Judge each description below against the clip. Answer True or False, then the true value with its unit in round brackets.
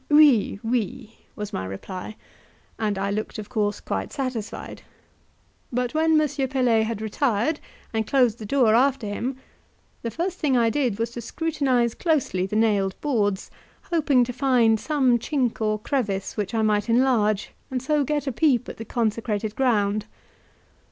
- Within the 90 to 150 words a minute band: False (160 wpm)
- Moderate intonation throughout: True (4.0 semitones)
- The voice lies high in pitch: True (235 Hz)